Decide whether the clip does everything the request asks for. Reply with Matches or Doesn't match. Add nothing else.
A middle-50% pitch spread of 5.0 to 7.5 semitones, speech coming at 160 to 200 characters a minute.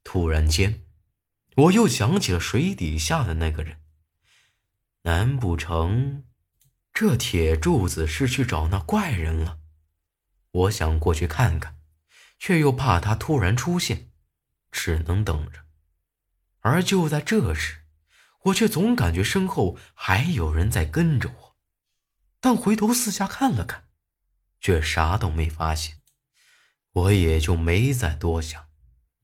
Doesn't match